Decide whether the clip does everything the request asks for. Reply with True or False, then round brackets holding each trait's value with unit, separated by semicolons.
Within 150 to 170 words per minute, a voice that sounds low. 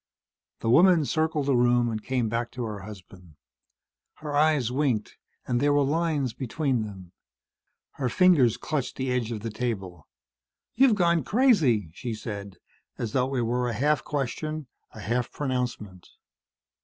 True (155 wpm; 125 Hz)